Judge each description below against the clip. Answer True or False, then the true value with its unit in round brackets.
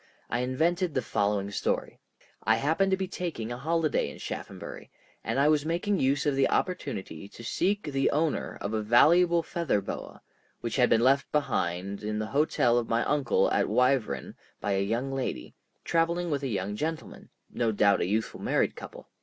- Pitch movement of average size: False (7.0 semitones)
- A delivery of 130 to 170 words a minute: False (180 wpm)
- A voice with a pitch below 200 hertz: True (135 Hz)